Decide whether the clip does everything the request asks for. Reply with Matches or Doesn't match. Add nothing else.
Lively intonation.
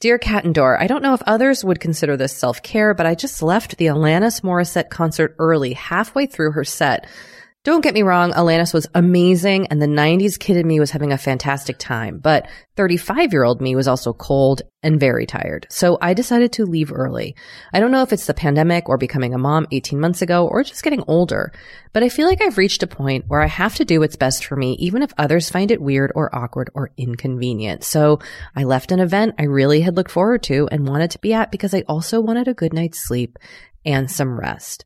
Matches